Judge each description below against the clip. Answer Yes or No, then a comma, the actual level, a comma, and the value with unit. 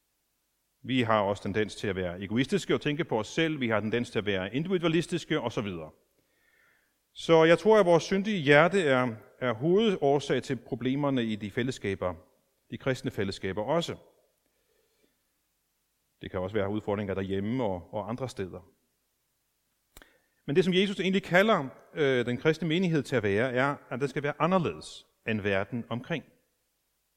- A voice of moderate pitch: No, low, 130 Hz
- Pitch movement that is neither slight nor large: No, wide, 7.6 semitones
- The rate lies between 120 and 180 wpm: Yes, average, 160 wpm